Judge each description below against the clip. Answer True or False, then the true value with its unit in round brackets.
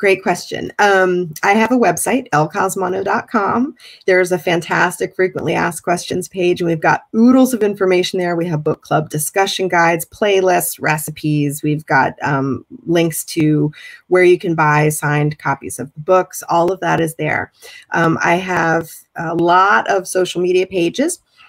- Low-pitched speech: False (175 Hz)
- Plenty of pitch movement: False (3.3 semitones)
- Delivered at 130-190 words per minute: True (160 wpm)